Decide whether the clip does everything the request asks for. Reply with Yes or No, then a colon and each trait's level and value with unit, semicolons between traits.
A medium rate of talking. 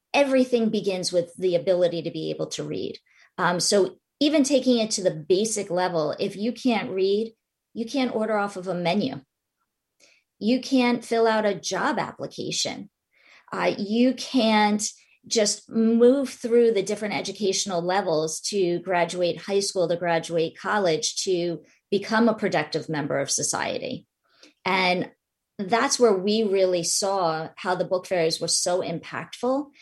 Yes: average, 150 wpm